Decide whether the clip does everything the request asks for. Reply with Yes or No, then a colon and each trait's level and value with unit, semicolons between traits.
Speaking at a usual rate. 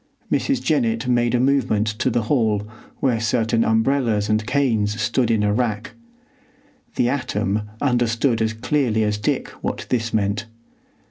Yes: average, 145 wpm